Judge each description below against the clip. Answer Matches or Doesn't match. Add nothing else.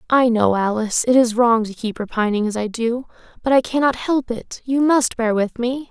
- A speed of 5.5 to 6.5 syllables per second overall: Doesn't match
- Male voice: Doesn't match